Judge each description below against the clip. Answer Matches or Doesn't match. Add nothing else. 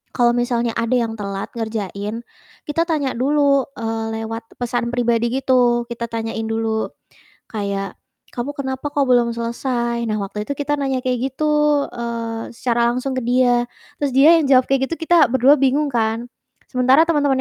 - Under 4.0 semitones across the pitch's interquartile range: Matches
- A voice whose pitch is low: Doesn't match